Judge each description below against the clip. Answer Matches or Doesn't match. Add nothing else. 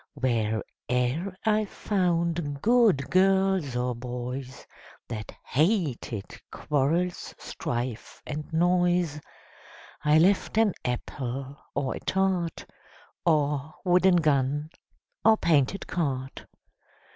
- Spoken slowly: Matches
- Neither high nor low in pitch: Matches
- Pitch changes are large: Matches